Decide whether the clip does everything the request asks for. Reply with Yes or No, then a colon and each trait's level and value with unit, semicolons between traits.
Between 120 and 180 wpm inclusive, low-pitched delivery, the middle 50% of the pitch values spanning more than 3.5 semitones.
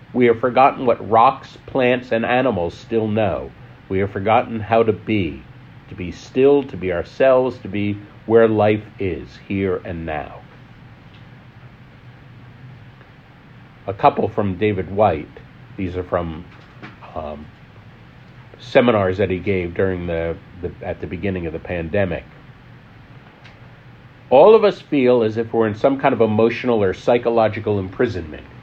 Yes: average, 140 wpm; low, 110 Hz; average, 4.7 semitones